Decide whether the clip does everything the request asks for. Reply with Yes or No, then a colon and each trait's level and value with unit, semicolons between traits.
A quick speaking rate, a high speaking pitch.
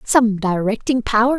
No: slow, 130 wpm; high, 225 Hz